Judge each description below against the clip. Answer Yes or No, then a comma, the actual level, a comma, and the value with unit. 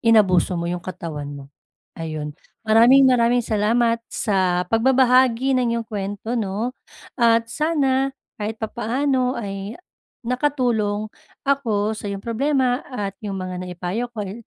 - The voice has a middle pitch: No, high, 225 Hz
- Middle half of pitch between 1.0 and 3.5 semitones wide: No, average, 4.1 semitones